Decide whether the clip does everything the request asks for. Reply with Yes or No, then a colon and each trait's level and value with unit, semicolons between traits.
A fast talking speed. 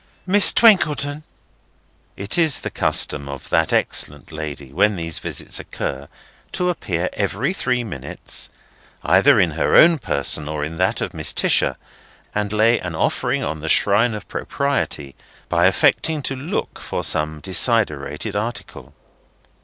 No: average, 145 wpm